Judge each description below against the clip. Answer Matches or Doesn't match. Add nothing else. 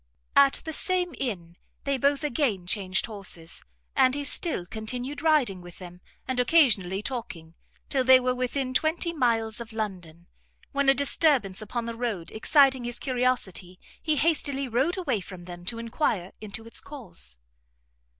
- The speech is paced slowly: Doesn't match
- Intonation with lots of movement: Matches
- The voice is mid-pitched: Doesn't match